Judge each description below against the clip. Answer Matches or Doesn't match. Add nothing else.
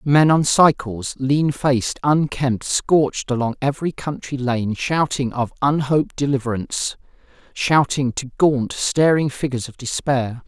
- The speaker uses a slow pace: Matches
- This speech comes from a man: Matches